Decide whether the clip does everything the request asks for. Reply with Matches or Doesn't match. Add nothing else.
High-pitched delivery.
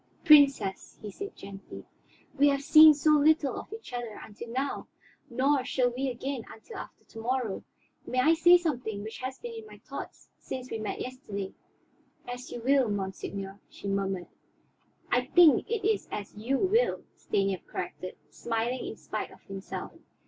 Matches